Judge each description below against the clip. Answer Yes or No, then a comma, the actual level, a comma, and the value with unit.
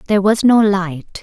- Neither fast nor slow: Yes, average, 195 wpm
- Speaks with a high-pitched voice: Yes, high, 200 Hz